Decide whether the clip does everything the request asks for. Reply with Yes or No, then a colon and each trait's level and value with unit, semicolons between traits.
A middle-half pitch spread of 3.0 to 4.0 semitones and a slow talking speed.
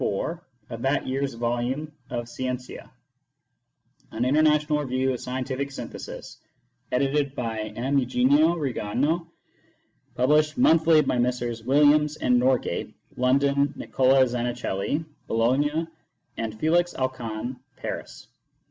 Yes: average, 3.3 semitones; slow, 110 wpm